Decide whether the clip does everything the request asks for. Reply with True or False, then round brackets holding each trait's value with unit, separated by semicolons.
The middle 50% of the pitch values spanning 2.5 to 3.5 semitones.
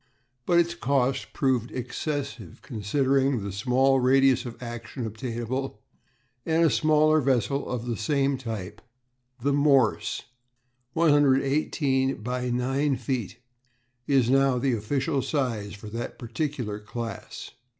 True (3.0 semitones)